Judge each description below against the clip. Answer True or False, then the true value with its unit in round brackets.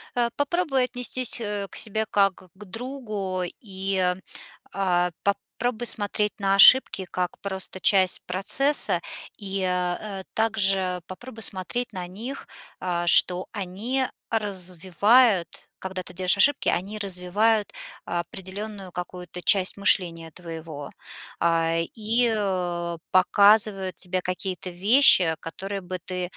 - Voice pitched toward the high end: True (195 Hz)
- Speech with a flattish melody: False (3.2 semitones)